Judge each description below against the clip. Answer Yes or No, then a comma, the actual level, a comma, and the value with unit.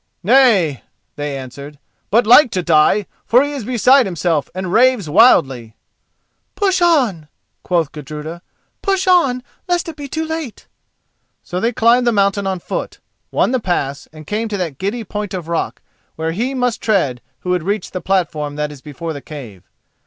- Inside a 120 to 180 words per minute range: Yes, average, 175 wpm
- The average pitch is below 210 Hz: Yes, high, 190 Hz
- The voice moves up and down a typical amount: No, wide, 8.2 semitones